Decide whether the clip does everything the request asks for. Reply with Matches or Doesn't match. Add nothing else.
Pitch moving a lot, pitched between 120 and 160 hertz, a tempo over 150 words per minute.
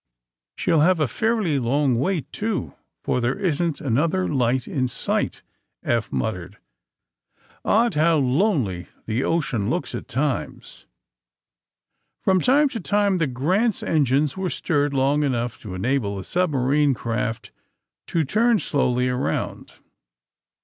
Doesn't match